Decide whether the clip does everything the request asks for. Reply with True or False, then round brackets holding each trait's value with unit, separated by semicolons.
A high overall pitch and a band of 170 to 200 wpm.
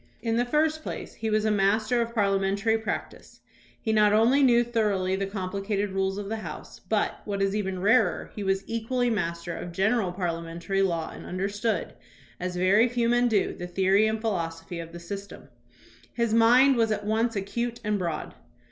True (205 Hz; 185 wpm)